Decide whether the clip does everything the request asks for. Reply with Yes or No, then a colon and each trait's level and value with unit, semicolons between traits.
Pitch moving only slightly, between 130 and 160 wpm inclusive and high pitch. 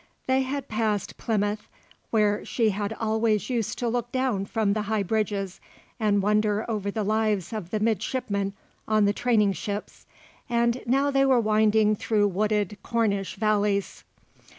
Yes: narrow, 2.0 semitones; average, 150 wpm; high, 215 Hz